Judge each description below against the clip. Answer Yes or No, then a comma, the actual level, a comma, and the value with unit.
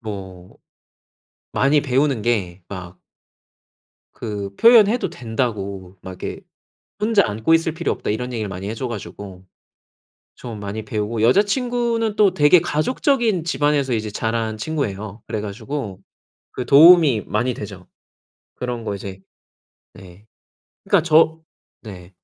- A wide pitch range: Yes, wide, 7.4 semitones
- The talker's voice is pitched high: No, low, 115 Hz